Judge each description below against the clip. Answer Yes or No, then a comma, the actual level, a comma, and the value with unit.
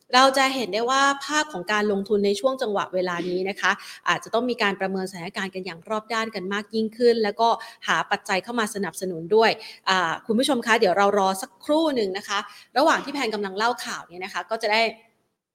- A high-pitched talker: Yes, high, 210 Hz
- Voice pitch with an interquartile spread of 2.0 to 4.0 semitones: Yes, average, 3.4 semitones